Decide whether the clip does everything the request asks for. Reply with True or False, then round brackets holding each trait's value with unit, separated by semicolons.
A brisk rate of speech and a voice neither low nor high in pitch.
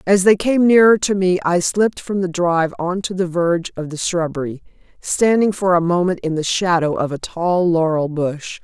True (210 wpm; 175 Hz)